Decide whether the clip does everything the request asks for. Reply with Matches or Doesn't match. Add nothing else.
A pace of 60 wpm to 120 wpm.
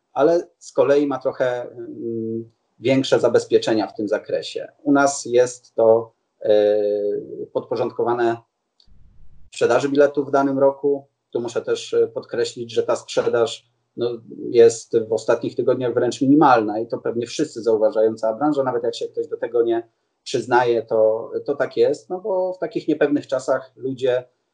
Doesn't match